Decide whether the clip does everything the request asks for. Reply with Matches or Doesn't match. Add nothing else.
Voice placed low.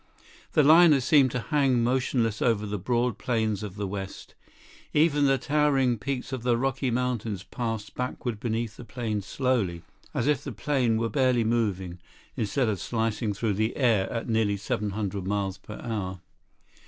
Matches